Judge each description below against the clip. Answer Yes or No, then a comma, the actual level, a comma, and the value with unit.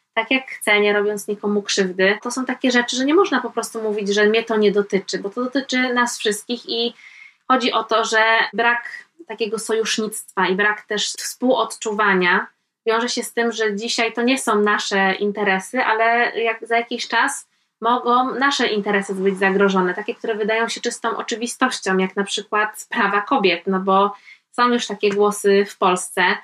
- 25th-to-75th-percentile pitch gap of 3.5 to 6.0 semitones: No, average, 2.7 semitones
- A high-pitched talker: Yes, high, 220 Hz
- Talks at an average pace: No, fast, 180 wpm